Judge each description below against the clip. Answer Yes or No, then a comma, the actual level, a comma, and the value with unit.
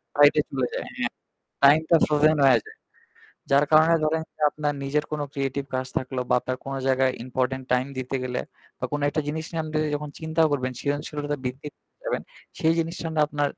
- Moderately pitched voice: Yes, medium, 145 Hz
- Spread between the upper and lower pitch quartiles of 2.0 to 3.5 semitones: Yes, average, 2.8 semitones